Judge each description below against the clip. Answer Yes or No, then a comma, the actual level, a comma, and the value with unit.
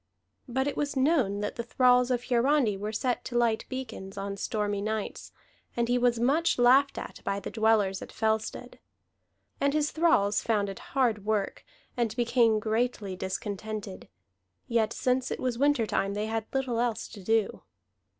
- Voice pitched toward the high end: Yes, high, 230 Hz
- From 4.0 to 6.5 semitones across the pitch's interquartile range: No, average, 3.2 semitones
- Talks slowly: No, average, 170 wpm